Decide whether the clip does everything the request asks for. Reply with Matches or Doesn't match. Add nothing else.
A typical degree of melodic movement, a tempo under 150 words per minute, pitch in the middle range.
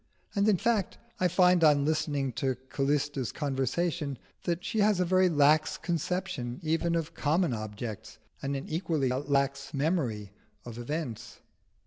Matches